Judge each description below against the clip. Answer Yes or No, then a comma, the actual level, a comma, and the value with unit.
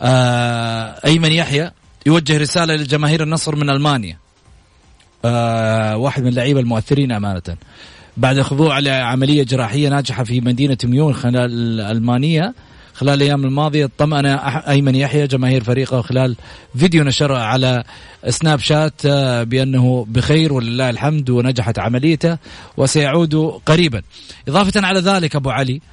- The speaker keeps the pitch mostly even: No, average, 3.5 semitones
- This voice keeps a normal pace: Yes, average, 125 wpm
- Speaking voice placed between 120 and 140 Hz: Yes, low, 135 Hz